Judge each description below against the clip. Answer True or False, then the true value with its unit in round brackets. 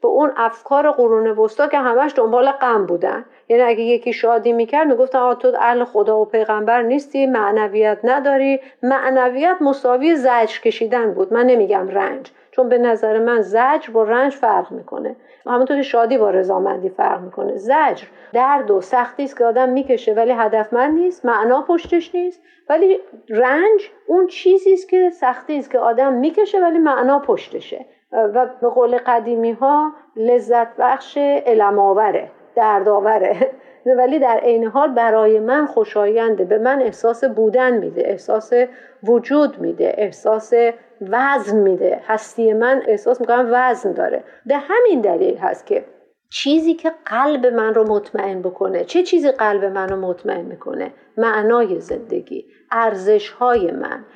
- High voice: True (245 Hz)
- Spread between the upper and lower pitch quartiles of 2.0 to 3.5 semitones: False (4.1 semitones)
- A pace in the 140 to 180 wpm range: True (150 wpm)